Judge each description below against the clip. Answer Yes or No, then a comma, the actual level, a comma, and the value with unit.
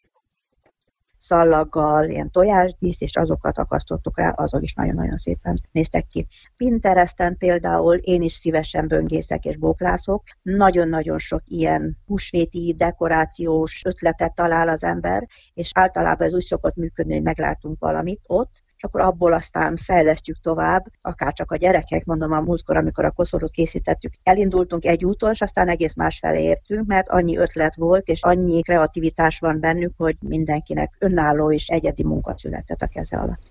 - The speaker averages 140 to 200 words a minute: Yes, average, 150 wpm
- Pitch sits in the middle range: Yes, medium, 165 Hz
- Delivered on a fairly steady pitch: No, average, 3.0 semitones